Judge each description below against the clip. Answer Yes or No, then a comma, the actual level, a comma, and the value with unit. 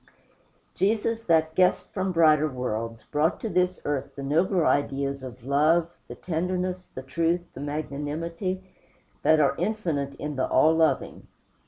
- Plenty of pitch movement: No, average, 4.4 semitones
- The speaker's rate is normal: Yes, average, 145 wpm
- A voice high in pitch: No, medium, 155 Hz